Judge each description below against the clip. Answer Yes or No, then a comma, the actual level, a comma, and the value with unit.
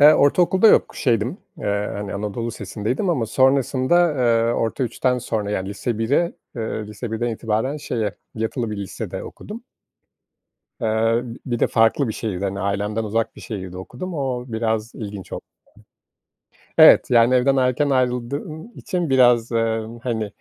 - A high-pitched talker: No, low, 115 Hz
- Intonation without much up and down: No, average, 3.4 semitones